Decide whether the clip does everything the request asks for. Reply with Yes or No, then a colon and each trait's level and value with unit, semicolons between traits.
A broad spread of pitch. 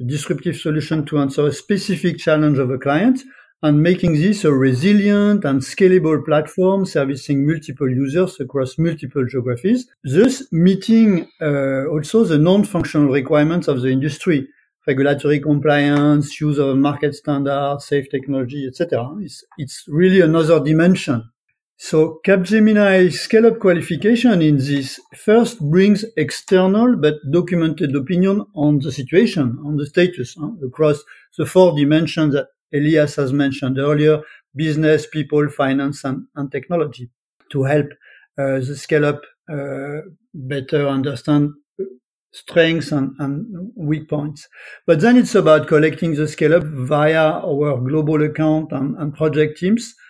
No: average, 3.7 semitones